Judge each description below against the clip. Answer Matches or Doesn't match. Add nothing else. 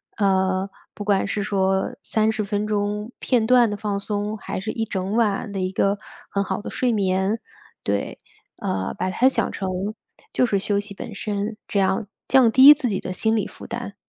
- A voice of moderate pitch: Doesn't match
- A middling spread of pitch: Doesn't match